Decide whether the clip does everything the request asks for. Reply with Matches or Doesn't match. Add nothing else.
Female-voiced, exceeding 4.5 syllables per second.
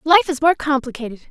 Matches